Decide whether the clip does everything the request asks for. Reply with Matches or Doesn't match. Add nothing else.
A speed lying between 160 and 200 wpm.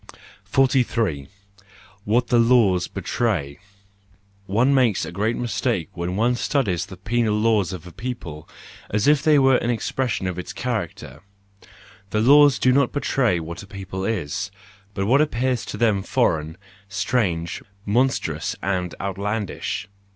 Doesn't match